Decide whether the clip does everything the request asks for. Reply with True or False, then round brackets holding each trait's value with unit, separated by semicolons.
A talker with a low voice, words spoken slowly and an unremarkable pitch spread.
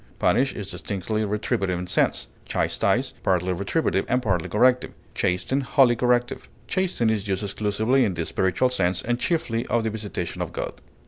False (110 Hz; 165 wpm; 4.5 semitones)